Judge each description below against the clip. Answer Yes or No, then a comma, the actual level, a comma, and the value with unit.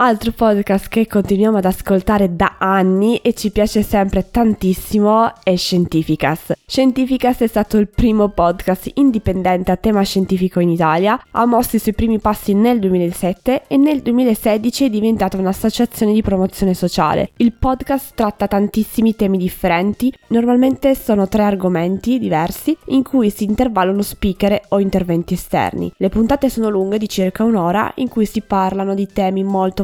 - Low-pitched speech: No, high, 205 Hz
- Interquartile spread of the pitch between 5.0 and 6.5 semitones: No, average, 3.4 semitones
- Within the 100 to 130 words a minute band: No, average, 155 wpm